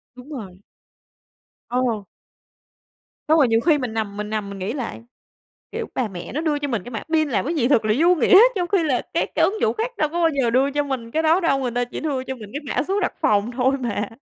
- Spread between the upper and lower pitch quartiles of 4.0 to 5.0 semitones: No, wide, 5.5 semitones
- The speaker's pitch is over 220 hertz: Yes, very high, 260 Hz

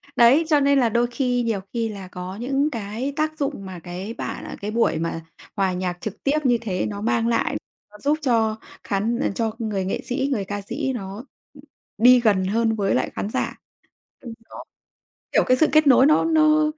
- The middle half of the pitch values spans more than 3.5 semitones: Yes, average, 5.1 semitones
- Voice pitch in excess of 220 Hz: Yes, high, 230 Hz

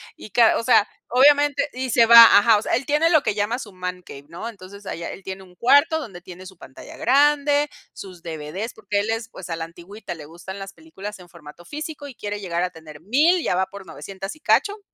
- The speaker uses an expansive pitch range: Yes, wide, 6.4 semitones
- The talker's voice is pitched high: Yes, high, 205 Hz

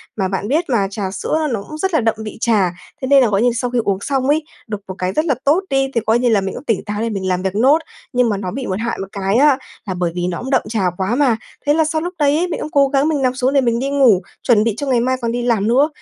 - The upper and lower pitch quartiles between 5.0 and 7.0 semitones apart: Yes, wide, 5.5 semitones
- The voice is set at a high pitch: Yes, high, 235 Hz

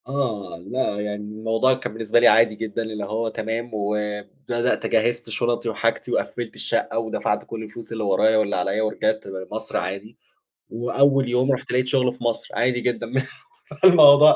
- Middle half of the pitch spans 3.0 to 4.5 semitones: No, narrow, 2.6 semitones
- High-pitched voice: No, low, 115 Hz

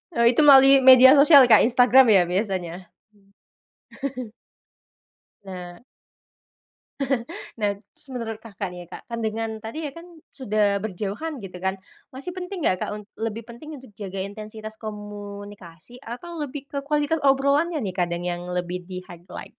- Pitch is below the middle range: No, high, 220 Hz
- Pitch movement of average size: No, wide, 6.1 semitones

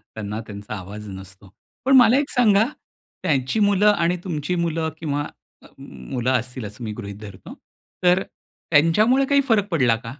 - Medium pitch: Yes, medium, 150 Hz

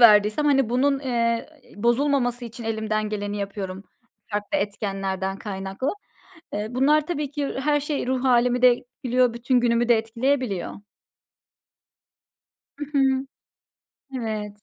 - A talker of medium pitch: No, high, 240 Hz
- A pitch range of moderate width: Yes, average, 4.1 semitones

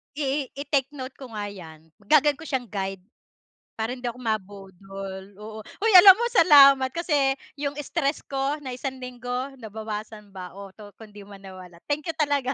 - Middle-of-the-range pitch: No, high, 245 Hz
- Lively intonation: Yes, wide, 5.8 semitones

